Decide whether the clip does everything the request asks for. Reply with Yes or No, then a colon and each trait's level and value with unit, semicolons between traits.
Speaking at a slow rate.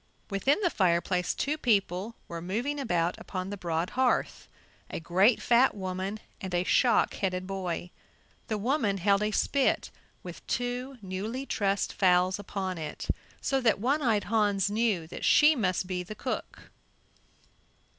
No: average, 150 wpm